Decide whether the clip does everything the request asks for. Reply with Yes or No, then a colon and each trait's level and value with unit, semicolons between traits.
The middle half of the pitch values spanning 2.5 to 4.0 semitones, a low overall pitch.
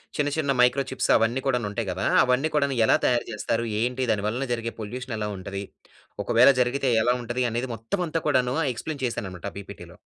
Yes: average, 2.8 semitones; low, 125 Hz